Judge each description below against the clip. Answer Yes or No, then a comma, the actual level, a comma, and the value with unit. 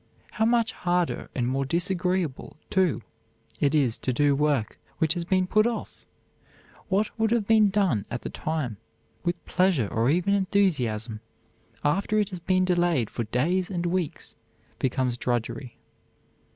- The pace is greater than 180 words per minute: No, average, 150 wpm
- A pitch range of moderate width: No, wide, 6.4 semitones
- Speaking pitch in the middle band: Yes, medium, 175 Hz